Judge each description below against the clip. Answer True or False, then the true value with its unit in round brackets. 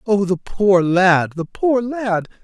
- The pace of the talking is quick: False (175 wpm)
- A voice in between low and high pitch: False (195 Hz)